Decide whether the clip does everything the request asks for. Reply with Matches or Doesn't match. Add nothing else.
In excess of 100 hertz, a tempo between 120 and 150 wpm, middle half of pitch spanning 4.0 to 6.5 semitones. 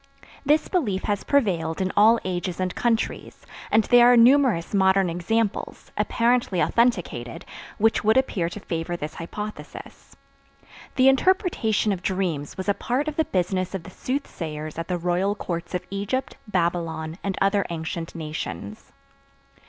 Matches